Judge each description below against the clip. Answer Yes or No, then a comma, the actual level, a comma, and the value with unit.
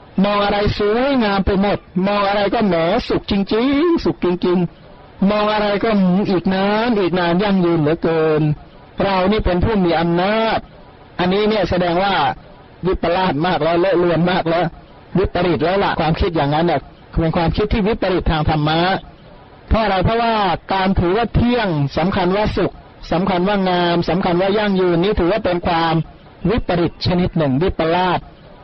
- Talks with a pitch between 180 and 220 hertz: Yes, medium, 185 Hz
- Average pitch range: Yes, average, 3.1 semitones